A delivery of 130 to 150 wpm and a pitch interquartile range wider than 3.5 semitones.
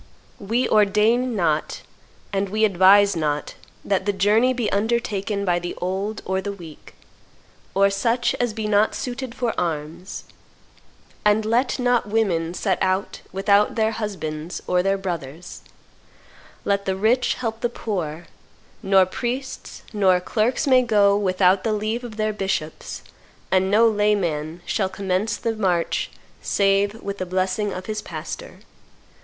No: average, 145 wpm; average, 2.9 semitones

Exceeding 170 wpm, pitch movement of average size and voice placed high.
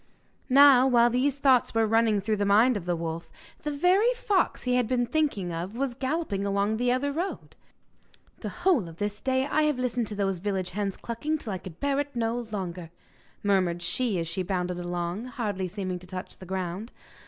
No: average, 200 wpm; wide, 5.8 semitones; high, 220 Hz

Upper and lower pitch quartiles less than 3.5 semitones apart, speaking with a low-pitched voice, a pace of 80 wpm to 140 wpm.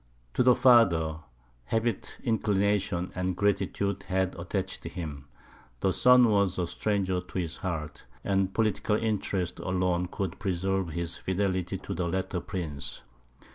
Yes: narrow, 2.4 semitones; very low, 95 Hz; slow, 135 wpm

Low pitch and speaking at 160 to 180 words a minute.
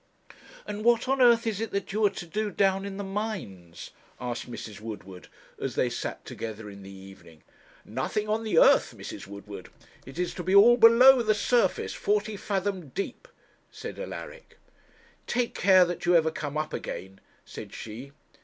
No: high, 190 Hz; average, 175 wpm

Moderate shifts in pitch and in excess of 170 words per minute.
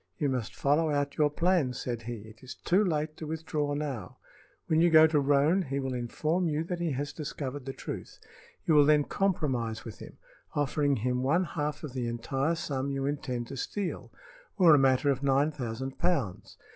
Yes: average, 3.3 semitones; average, 195 wpm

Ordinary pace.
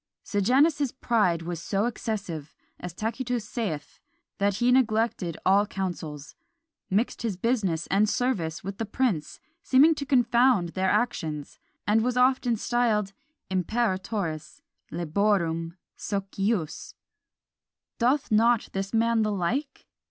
No: slow, 115 wpm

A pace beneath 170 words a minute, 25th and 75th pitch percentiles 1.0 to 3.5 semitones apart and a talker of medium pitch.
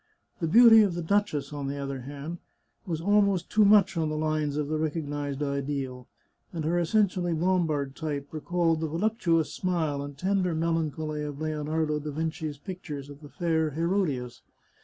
Yes: average, 160 wpm; average, 3.2 semitones; medium, 155 Hz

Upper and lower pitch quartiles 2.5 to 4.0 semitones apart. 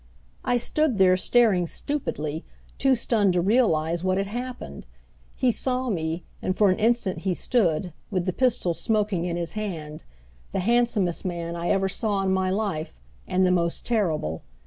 No: average, 4.9 semitones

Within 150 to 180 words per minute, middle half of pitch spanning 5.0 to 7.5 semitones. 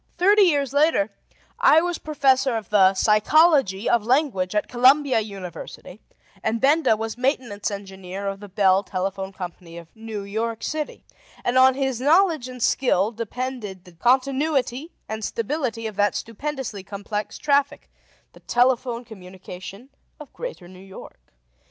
No: average, 140 wpm; wide, 5.4 semitones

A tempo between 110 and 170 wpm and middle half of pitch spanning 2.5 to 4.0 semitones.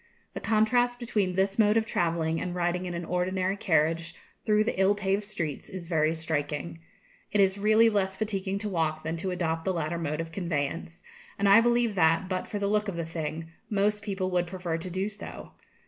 No: fast, 205 wpm; average, 3.7 semitones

